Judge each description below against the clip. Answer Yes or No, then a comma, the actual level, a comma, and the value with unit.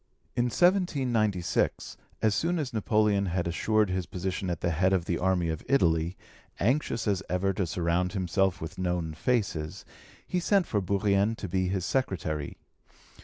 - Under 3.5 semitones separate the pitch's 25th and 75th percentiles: No, average, 3.8 semitones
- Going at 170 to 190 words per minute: No, average, 160 wpm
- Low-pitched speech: Yes, very low, 95 Hz